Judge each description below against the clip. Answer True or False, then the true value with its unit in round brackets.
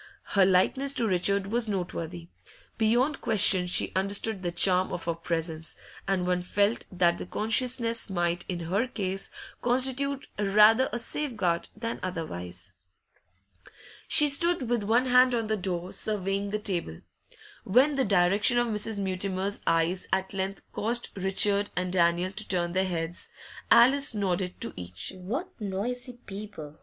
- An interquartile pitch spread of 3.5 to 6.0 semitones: True (4.4 semitones)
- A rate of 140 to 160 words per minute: True (150 wpm)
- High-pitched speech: True (195 Hz)